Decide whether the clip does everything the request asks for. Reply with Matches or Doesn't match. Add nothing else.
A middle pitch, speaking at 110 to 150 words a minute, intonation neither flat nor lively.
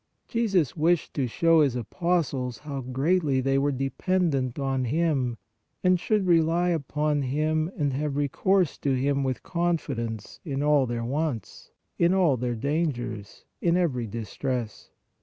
Matches